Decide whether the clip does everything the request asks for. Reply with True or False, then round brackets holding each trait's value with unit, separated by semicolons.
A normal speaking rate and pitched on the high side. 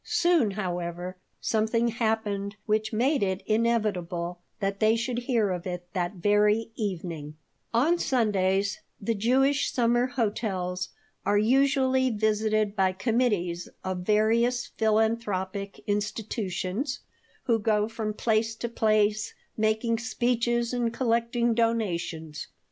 False (115 wpm; 215 Hz)